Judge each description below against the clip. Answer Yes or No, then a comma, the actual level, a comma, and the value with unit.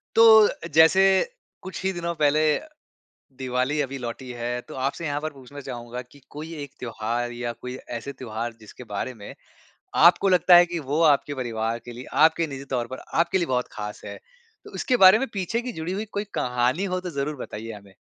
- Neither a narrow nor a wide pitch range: No, wide, 5.9 semitones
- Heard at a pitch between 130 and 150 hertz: Yes, medium, 140 Hz